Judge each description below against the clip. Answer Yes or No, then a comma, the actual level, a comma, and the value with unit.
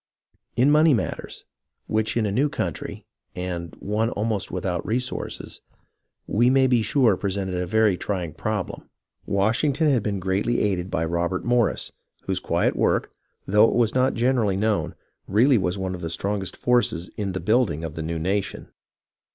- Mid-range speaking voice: No, low, 105 Hz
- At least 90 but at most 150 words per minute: No, average, 165 wpm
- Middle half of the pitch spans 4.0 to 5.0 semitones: Yes, average, 4.5 semitones